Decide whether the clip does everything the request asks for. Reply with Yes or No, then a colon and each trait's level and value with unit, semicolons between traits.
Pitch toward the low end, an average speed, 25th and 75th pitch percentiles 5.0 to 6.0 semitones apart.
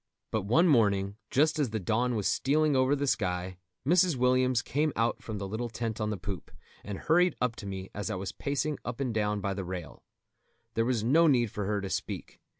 No: low, 115 Hz; fast, 220 wpm; wide, 5.4 semitones